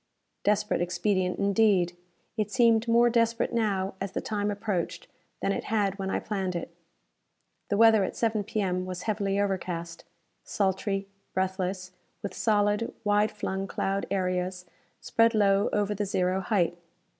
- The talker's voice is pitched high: Yes, high, 200 Hz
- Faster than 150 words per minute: No, average, 145 wpm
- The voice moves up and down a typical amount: No, narrow, 2.3 semitones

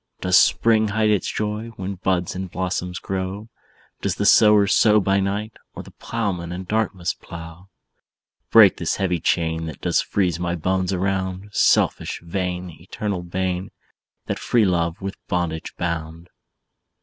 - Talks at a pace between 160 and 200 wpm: No, average, 150 wpm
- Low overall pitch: Yes, very low, 95 Hz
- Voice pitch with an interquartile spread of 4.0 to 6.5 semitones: No, narrow, 2.5 semitones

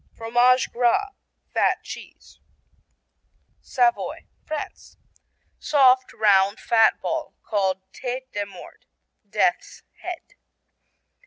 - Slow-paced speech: Yes, slow, 85 wpm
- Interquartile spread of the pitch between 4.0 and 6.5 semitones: No, average, 3.6 semitones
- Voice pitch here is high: Yes, high, 245 Hz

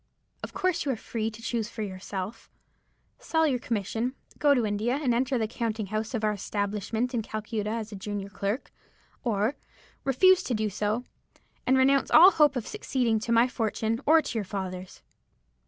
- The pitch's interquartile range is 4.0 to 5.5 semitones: No, average, 3.6 semitones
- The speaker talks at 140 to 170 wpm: No, average, 180 wpm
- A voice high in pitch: Yes, high, 225 Hz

